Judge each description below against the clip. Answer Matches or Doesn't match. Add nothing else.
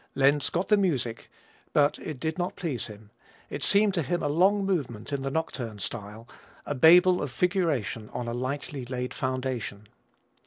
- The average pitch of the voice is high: Doesn't match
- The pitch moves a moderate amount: Doesn't match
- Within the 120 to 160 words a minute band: Doesn't match